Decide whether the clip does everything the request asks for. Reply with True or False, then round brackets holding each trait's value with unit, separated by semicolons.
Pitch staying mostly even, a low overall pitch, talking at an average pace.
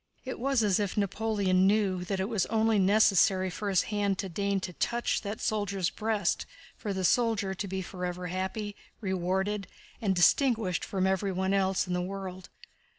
False (2.1 semitones; 195 Hz; 170 wpm)